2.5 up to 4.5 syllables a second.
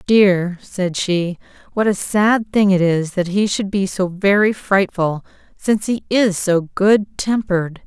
Yes: 3.9 syllables/s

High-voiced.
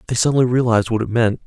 No: low, 115 Hz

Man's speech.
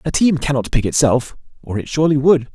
Yes: male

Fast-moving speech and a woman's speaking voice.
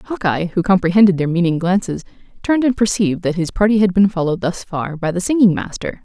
Yes: fast, 210 wpm; female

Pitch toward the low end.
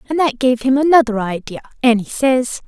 No: very high, 250 Hz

